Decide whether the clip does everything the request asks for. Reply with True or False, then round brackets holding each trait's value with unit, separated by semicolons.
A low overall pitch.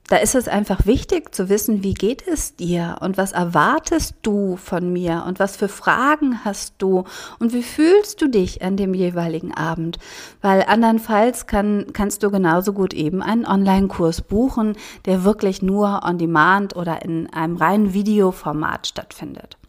False (195 Hz)